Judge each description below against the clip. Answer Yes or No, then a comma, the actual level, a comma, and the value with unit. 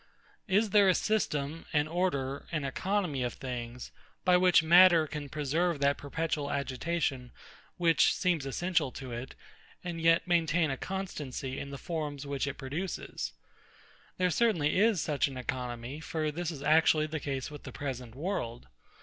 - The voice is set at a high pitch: No, medium, 150 Hz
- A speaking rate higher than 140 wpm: Yes, average, 160 wpm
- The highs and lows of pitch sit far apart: No, average, 4.3 semitones